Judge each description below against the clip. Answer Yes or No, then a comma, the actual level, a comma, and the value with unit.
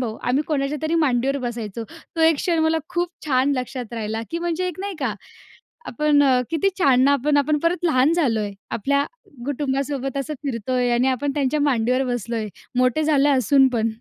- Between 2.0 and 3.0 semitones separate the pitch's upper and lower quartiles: No, average, 3.5 semitones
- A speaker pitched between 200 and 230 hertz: No, very high, 275 Hz